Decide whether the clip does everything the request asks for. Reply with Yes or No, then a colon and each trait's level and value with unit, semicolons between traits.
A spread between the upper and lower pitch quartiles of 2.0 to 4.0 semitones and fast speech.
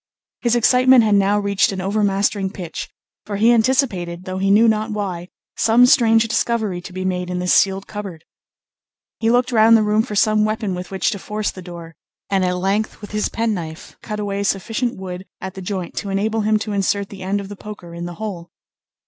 Yes: average, 2.7 semitones; fast, 210 wpm